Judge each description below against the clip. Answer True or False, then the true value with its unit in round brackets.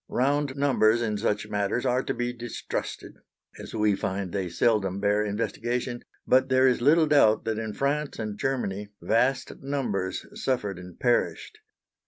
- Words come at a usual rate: True (155 wpm)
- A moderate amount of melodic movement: True (4.2 semitones)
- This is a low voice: True (115 Hz)